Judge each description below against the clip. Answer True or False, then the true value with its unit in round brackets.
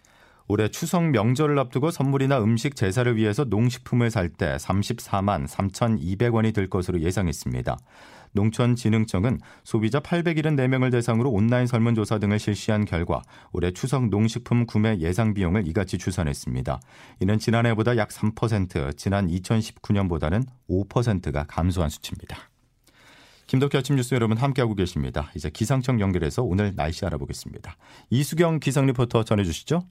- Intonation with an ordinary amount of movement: True (4.8 semitones)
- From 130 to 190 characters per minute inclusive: False (335 characters per minute)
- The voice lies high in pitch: False (110 Hz)